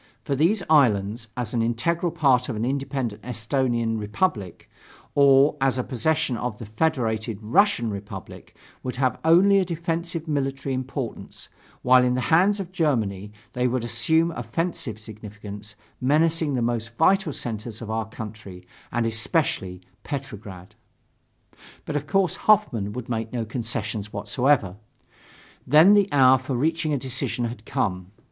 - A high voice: No, low, 125 Hz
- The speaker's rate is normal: Yes, average, 145 wpm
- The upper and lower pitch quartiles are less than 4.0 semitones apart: No, wide, 5.6 semitones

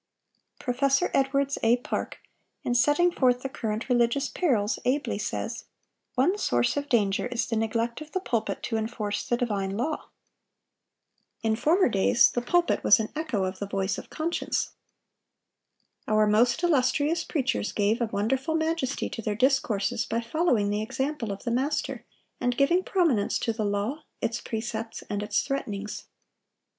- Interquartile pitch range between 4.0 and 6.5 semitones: Yes, average, 4.5 semitones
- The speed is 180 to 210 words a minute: No, average, 155 wpm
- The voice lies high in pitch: Yes, high, 240 Hz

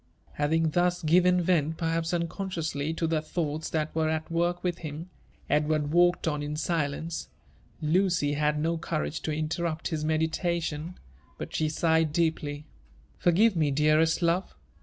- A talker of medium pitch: Yes, medium, 160 Hz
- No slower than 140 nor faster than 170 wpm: Yes, average, 145 wpm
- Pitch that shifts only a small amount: Yes, narrow, 2.1 semitones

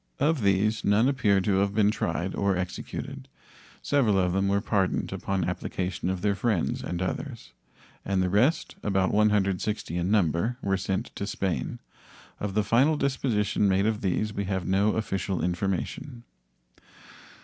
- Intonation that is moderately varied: No, narrow, 2.3 semitones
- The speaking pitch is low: Yes, low, 100 Hz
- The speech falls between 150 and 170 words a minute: Yes, average, 155 wpm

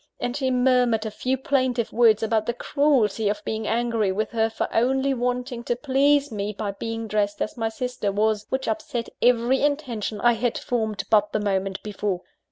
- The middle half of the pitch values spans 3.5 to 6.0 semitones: No, average, 3.0 semitones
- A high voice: Yes, high, 230 Hz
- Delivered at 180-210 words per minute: Yes, average, 185 wpm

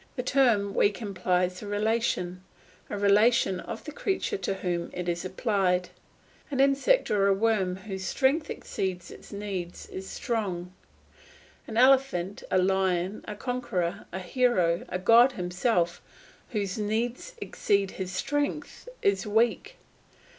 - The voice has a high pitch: Yes, high, 200 Hz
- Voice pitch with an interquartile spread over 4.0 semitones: Yes, average, 4.5 semitones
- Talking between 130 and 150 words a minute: Yes, slow, 135 wpm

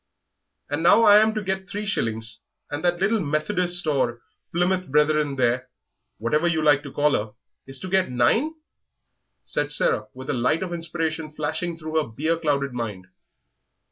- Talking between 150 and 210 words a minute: Yes, average, 170 wpm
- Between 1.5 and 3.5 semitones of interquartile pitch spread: No, average, 5.0 semitones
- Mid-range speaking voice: Yes, medium, 155 Hz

